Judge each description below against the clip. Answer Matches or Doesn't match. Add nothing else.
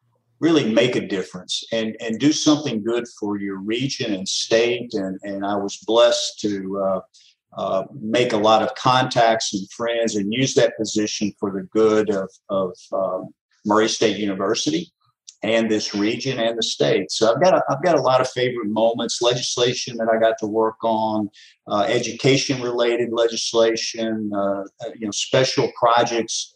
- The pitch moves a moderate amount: Doesn't match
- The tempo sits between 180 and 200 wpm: Doesn't match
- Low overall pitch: Matches